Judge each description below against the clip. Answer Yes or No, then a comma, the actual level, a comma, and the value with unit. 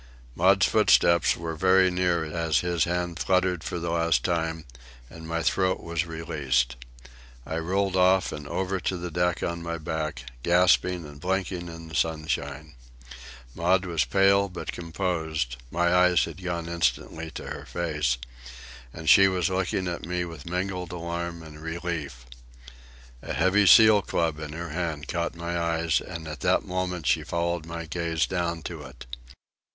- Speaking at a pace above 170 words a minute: No, average, 155 wpm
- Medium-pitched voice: No, very low, 85 Hz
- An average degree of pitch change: No, narrow, 2.0 semitones